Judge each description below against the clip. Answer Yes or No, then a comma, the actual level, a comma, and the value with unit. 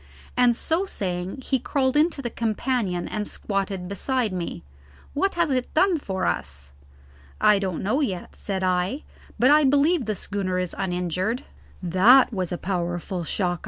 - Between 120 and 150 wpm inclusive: No, average, 160 wpm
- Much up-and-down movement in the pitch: Yes, wide, 6.5 semitones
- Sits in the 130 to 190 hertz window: No, high, 200 Hz